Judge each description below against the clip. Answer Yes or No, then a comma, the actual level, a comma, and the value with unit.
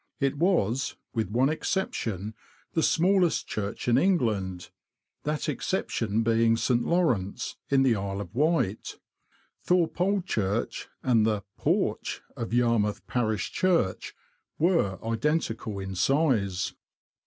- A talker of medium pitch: No, low, 115 Hz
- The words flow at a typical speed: No, slow, 120 wpm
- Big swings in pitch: Yes, wide, 7.1 semitones